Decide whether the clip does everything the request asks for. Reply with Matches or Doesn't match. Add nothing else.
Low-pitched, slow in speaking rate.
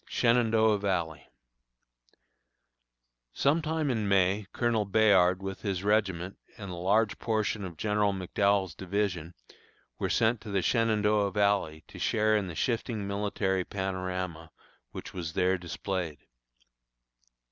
Matches